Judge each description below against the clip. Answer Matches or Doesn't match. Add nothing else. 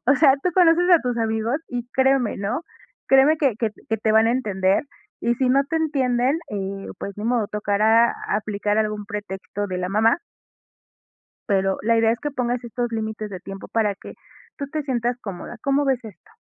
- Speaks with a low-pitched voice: Doesn't match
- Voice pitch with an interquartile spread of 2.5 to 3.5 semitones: Doesn't match